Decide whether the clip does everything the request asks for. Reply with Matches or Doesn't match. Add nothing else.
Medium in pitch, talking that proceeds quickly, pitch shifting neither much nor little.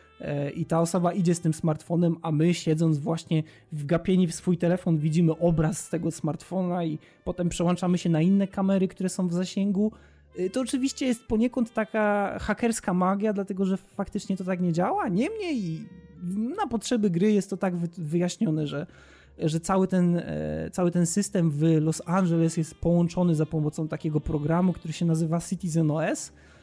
Matches